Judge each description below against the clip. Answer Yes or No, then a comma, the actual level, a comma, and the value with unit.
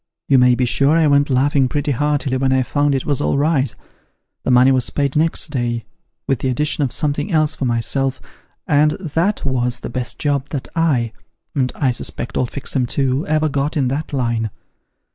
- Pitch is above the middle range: No, medium, 140 Hz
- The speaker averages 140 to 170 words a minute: No, average, 195 wpm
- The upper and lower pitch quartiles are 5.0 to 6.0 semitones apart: No, narrow, 2.6 semitones